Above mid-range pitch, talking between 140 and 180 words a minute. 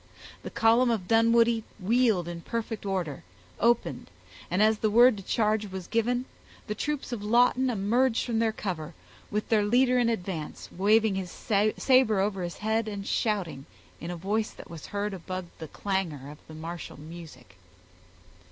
Yes: high, 210 Hz; average, 165 wpm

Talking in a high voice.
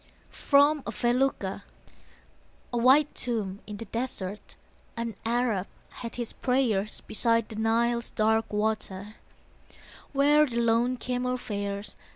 Yes: high, 230 Hz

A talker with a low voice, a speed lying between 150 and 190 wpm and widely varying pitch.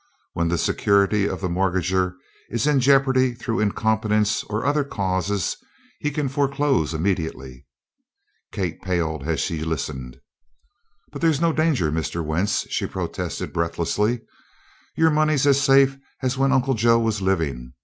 No: low, 105 Hz; average, 140 wpm; wide, 8.1 semitones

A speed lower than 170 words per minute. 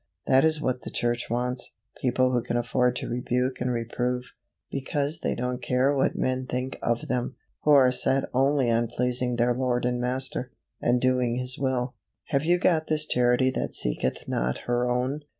No: average, 185 wpm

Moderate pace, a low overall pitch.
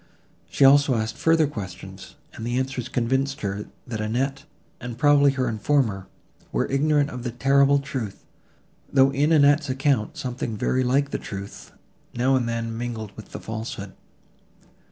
Yes: average, 155 wpm; low, 130 Hz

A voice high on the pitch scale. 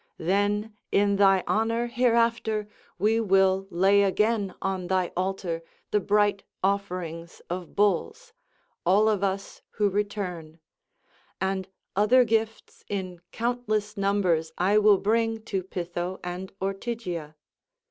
Yes: high, 200 Hz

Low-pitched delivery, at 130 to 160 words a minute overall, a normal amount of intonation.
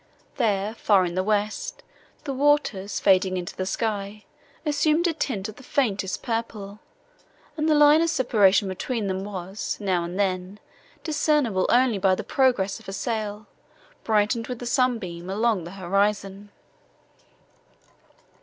No: high, 210 Hz; average, 145 wpm; average, 4.6 semitones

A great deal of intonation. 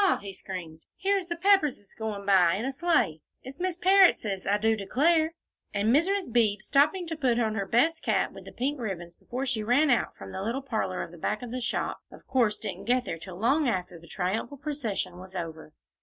Yes: wide, 7.1 semitones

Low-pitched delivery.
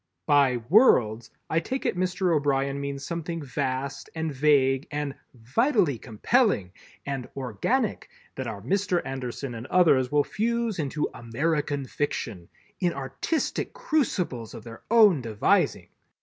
No: medium, 145 Hz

